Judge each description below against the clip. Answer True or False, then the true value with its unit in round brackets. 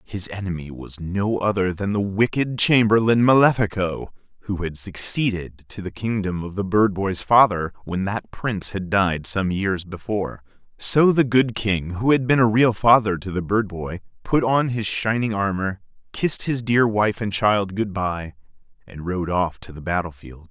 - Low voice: True (100 Hz)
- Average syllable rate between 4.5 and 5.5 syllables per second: True (4.6 syllables/s)